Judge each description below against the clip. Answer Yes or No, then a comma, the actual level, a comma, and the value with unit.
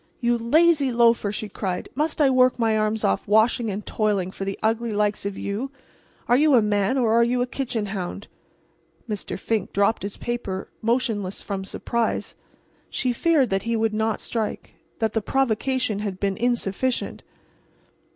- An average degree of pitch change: Yes, average, 3.2 semitones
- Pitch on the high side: Yes, high, 225 Hz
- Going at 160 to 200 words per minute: Yes, average, 165 wpm